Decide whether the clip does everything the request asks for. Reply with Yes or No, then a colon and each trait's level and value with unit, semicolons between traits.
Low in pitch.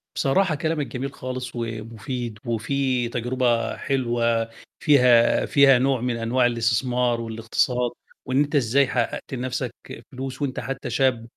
Yes: low, 125 Hz